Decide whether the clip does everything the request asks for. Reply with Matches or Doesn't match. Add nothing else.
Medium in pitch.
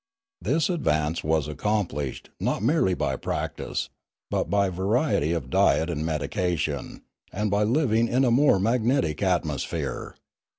Doesn't match